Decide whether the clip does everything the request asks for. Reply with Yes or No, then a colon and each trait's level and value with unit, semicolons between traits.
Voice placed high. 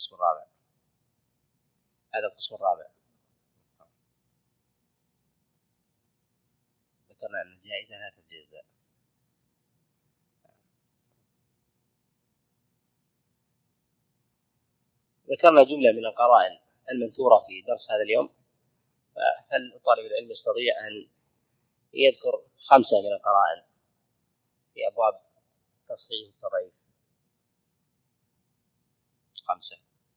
No: medium, 170 Hz